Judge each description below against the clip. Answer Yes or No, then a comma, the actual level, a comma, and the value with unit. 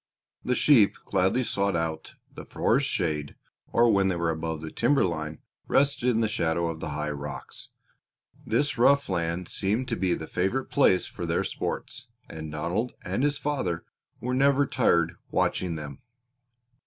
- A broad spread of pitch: Yes, wide, 7.4 semitones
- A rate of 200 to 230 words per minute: No, average, 165 wpm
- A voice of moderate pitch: No, very low, 95 Hz